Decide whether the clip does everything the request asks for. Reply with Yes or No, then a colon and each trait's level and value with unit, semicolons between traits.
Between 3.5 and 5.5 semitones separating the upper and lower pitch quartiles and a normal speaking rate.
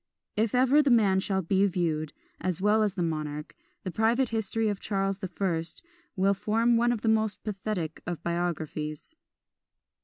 Yes: average, 4.3 semitones; average, 165 wpm